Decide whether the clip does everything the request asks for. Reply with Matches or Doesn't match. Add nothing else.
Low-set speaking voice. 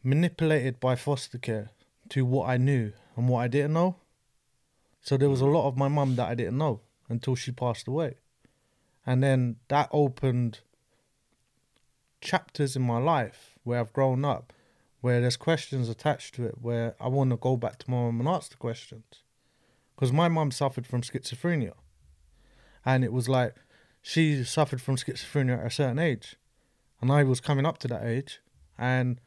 Matches